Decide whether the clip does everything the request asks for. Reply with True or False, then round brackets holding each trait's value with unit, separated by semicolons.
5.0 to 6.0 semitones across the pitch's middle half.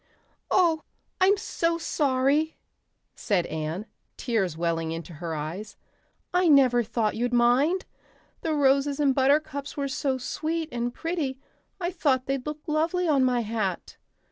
True (5.4 semitones)